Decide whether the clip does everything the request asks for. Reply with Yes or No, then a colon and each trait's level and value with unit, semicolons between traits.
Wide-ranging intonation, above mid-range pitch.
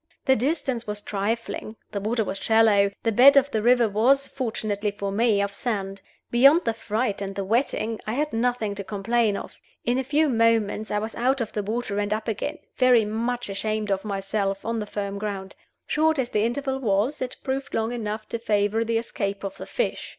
No: average, 3.1 semitones; high, 220 Hz